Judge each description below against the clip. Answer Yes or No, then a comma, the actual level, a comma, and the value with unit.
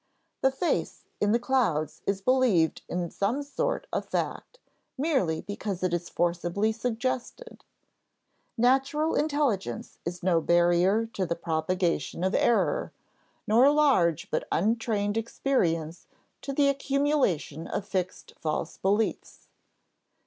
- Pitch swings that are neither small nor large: No, wide, 7.4 semitones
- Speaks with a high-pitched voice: Yes, high, 205 Hz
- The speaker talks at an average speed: No, slow, 120 wpm